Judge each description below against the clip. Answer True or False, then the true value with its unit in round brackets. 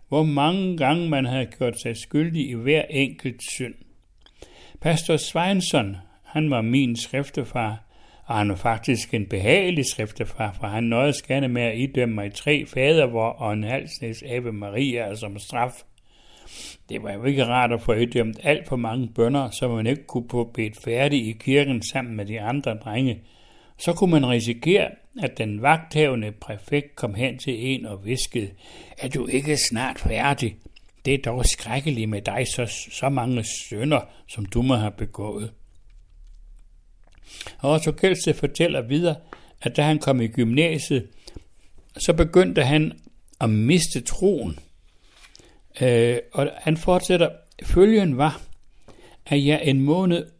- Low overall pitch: True (125 Hz)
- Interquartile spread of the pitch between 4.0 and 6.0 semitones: True (4.5 semitones)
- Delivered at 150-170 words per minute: True (155 wpm)